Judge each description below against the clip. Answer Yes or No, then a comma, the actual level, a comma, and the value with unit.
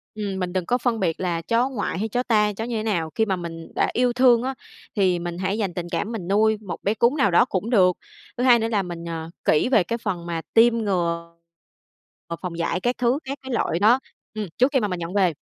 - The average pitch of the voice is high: Yes, high, 205 Hz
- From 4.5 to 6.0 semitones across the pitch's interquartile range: Yes, average, 5.1 semitones